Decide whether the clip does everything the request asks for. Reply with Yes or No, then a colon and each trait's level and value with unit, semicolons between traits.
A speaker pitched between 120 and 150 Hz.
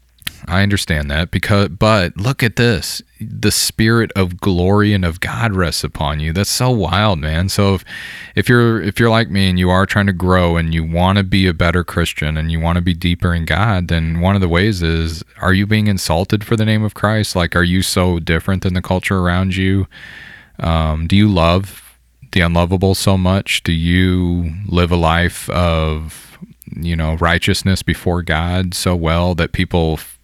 No: very low, 90 Hz